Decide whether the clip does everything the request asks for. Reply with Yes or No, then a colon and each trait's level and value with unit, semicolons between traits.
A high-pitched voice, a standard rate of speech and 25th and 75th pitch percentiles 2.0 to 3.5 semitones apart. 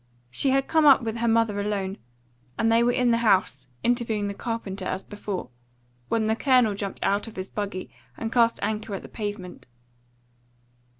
Yes: high, 220 Hz; average, 180 wpm; average, 2.7 semitones